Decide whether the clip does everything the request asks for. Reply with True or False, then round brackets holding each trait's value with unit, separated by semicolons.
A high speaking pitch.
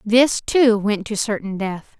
True (215 Hz)